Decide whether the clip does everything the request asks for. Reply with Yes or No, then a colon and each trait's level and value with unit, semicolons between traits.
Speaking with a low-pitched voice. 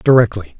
Yes: low, 110 Hz